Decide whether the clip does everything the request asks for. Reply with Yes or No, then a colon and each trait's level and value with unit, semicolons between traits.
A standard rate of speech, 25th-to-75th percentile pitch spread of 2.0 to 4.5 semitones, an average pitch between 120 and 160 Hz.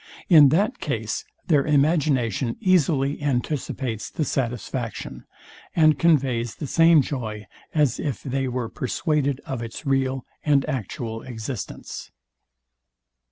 No: slow, 115 wpm; average, 3.7 semitones; low, 135 Hz